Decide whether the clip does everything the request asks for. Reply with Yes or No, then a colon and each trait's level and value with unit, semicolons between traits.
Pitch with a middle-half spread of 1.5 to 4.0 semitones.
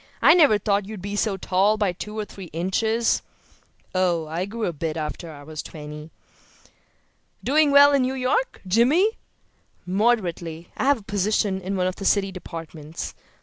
No: average, 5.0 semitones